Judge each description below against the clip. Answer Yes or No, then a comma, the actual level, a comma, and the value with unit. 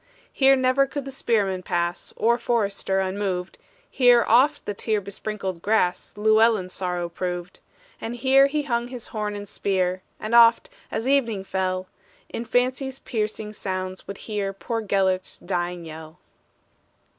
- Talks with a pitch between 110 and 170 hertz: No, high, 210 Hz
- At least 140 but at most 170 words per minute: Yes, average, 145 wpm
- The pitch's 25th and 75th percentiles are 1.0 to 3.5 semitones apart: No, average, 4.3 semitones